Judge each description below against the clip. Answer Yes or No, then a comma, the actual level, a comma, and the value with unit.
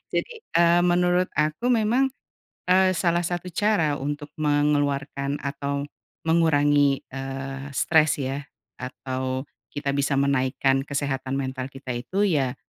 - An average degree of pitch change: Yes, average, 3.6 semitones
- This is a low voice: No, medium, 145 Hz